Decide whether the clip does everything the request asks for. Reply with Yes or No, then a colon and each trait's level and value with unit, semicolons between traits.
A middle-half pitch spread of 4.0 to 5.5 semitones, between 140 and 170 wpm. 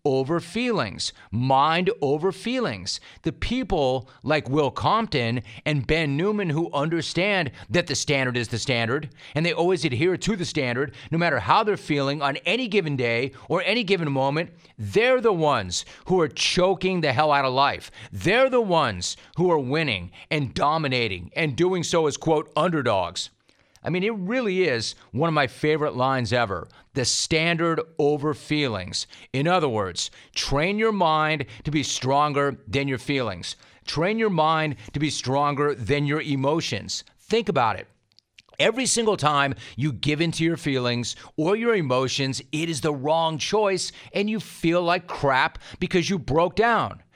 Yes: average, 4.9 semitones; average, 165 wpm